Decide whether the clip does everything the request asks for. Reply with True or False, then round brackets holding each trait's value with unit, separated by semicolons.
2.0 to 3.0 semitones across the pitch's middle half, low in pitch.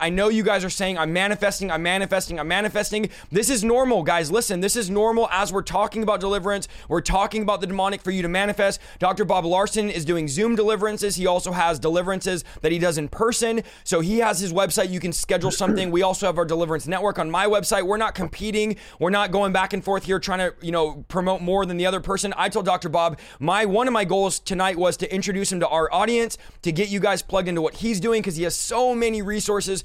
False (2.7 semitones; 195 Hz)